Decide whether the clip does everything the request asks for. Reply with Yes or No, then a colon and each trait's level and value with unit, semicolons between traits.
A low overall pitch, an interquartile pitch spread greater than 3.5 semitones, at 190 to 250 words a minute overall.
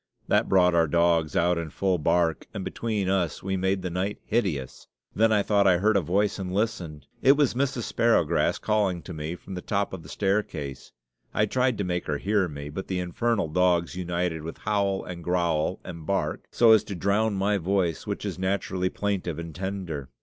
No: very low, 95 Hz; average, 3.1 semitones; average, 200 wpm